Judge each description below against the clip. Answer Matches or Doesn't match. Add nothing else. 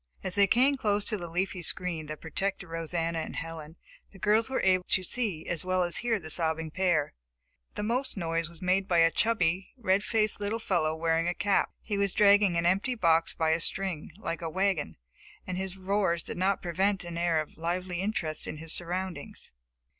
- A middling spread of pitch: Matches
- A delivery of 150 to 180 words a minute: Doesn't match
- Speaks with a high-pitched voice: Doesn't match